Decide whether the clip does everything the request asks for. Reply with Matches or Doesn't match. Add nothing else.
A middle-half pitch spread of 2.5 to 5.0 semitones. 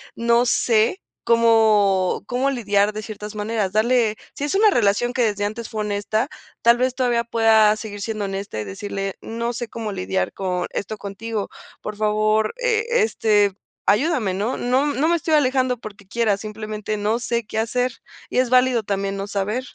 Matches